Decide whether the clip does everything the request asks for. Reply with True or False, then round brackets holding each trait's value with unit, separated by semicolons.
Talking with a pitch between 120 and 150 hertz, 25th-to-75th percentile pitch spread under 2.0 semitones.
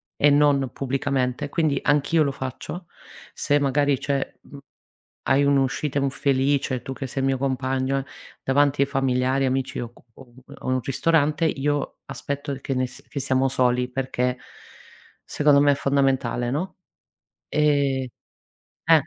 True (135 Hz; 1.5 semitones)